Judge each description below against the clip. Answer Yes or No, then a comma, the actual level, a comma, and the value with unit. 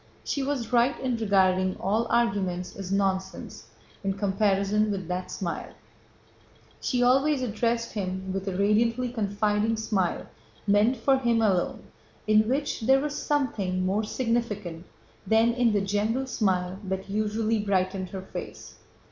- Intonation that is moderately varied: Yes, average, 3.5 semitones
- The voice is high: Yes, high, 210 Hz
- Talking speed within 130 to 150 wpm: Yes, average, 140 wpm